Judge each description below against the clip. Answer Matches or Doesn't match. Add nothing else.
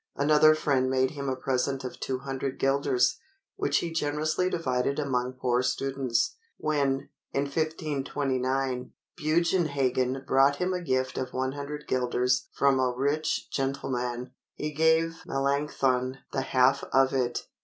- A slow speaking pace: Matches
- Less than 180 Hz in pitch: Matches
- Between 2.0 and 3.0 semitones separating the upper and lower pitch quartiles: Matches